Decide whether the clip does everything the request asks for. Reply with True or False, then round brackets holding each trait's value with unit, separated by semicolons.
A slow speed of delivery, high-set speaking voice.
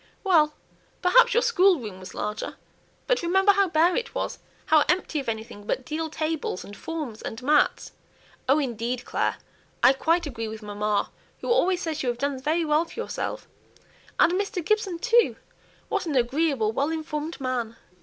False (170 wpm; 305 Hz)